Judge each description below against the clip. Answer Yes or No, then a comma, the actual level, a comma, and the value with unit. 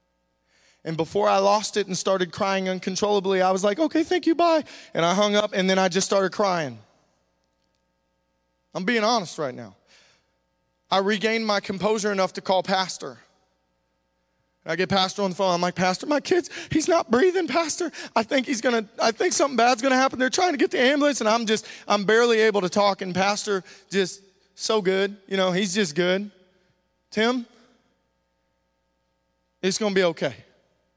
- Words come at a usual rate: Yes, average, 180 wpm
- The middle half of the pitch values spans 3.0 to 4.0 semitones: No, average, 5.3 semitones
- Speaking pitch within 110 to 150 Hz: No, high, 195 Hz